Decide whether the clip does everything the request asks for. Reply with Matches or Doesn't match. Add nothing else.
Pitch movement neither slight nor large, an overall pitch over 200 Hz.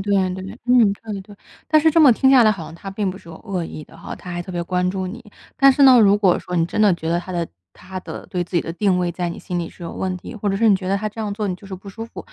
Doesn't match